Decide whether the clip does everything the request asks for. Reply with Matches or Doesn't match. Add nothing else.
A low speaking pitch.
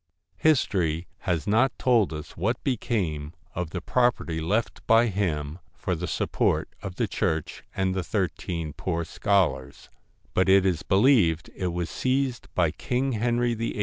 Matches